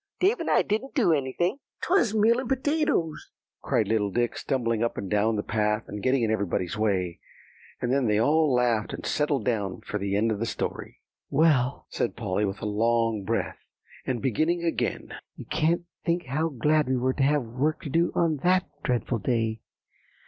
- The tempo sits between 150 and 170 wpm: No, average, 190 wpm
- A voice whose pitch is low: Yes, low, 125 Hz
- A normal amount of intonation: No, wide, 6.7 semitones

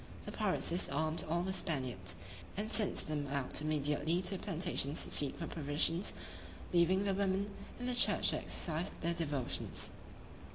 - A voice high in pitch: No, medium, 165 Hz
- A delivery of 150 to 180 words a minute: Yes, average, 160 wpm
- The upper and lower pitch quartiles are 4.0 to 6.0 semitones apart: Yes, average, 4.4 semitones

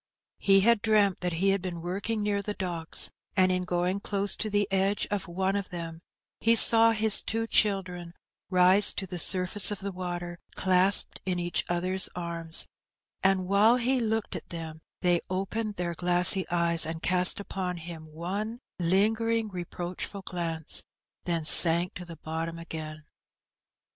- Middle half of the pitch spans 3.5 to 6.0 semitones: No, average, 2.7 semitones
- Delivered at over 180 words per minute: No, average, 160 wpm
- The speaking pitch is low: No, medium, 185 Hz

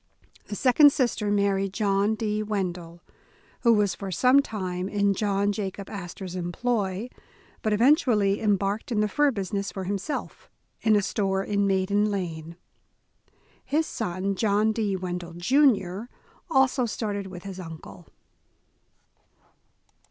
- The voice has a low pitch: No, high, 200 Hz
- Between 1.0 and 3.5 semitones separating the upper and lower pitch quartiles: Yes, narrow, 2.6 semitones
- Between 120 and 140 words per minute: Yes, slow, 135 wpm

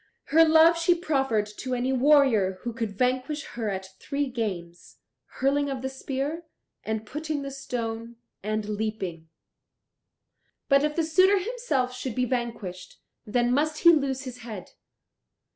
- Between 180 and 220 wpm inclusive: No, average, 145 wpm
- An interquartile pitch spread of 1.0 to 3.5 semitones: No, average, 5.0 semitones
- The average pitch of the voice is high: Yes, very high, 255 Hz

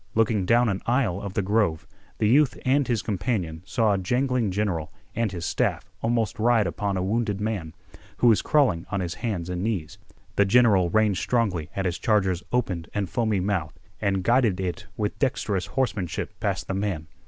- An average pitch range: Yes, average, 3.9 semitones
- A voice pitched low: Yes, low, 105 Hz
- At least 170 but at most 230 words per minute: Yes, average, 185 wpm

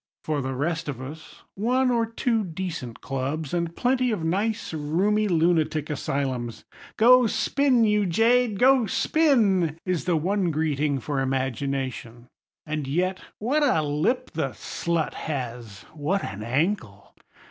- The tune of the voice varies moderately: No, wide, 7.2 semitones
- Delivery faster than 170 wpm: No, slow, 135 wpm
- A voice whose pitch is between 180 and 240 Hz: No, medium, 165 Hz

